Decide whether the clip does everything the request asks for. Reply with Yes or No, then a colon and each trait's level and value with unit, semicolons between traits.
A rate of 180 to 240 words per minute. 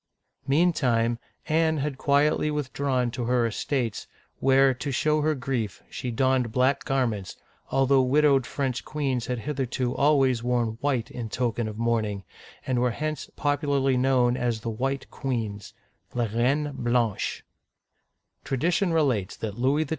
No: average, 145 wpm